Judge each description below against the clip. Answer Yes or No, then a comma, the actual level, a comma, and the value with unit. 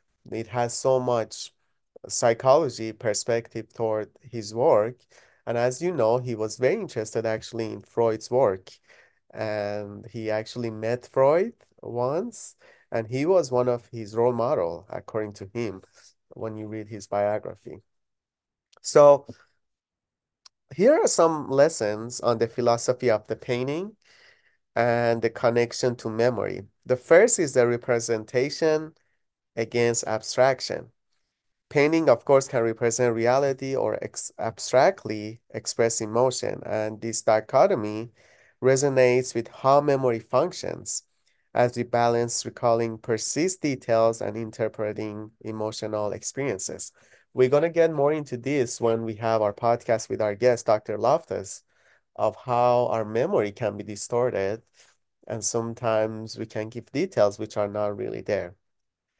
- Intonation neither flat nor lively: No, narrow, 2.3 semitones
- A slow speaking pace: Yes, slow, 130 wpm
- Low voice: Yes, low, 115 Hz